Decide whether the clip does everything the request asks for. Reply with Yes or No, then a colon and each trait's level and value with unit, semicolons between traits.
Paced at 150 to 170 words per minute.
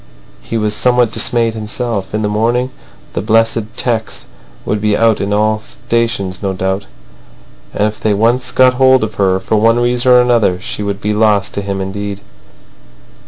No: average, 180 wpm